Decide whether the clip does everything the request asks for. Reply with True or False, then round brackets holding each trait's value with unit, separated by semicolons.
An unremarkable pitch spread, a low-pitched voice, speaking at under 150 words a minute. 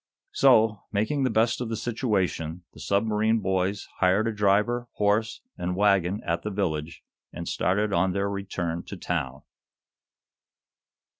True (3.1 semitones; 100 Hz; 140 wpm)